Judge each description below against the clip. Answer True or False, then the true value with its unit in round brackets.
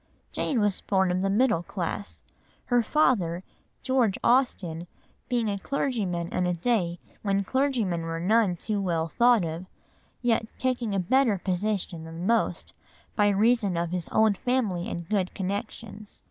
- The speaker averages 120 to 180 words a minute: True (150 wpm)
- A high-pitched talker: True (200 Hz)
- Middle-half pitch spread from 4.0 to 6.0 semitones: True (4.7 semitones)